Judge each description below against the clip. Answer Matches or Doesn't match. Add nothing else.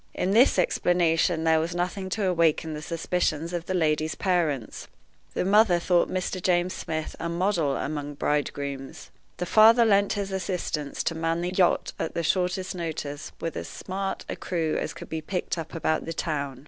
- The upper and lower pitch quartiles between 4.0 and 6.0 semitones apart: Doesn't match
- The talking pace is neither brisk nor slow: Matches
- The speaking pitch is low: Doesn't match